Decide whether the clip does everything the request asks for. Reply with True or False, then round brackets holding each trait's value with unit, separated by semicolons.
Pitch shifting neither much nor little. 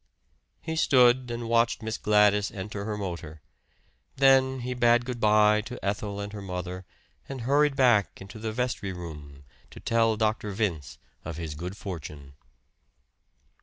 True (4.4 semitones)